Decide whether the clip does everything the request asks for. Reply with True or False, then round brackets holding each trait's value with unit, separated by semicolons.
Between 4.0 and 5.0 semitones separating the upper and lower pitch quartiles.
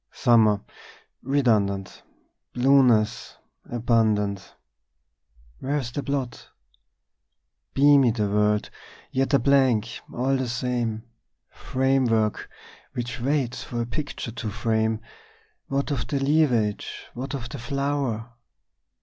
False (3.6 semitones)